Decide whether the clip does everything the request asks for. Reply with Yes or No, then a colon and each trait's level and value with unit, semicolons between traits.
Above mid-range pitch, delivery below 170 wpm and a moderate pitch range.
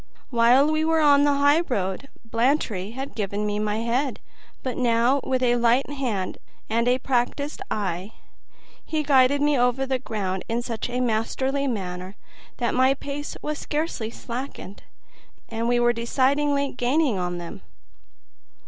Yes: high, 245 Hz; average, 150 wpm; average, 3.9 semitones